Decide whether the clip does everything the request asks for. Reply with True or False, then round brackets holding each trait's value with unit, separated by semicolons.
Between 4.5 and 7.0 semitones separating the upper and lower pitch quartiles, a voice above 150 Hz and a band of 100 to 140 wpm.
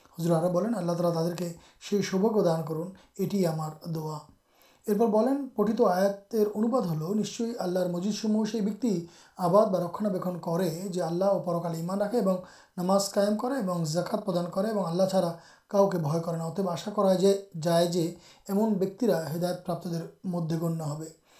False (3.2 semitones; 185 Hz; 110 wpm)